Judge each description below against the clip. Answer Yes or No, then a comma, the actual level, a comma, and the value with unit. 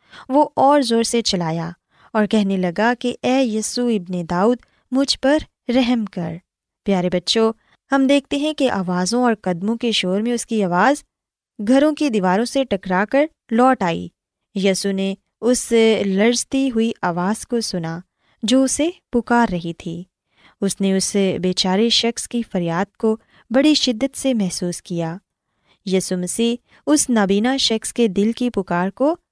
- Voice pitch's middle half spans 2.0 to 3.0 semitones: No, average, 5.0 semitones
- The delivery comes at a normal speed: Yes, average, 160 wpm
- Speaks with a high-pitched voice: Yes, high, 220 Hz